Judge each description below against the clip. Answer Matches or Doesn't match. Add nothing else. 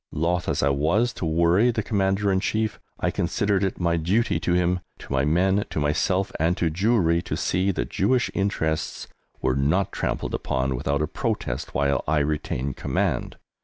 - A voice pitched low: Matches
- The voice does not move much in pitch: Doesn't match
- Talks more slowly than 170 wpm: Doesn't match